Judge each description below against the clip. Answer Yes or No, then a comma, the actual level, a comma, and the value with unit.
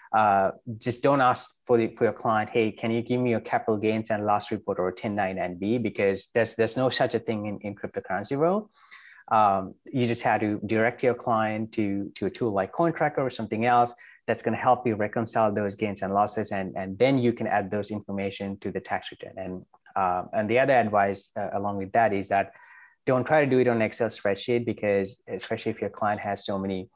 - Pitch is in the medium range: No, low, 110 Hz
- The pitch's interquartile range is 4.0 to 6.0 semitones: No, average, 2.9 semitones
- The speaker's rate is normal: No, fast, 225 wpm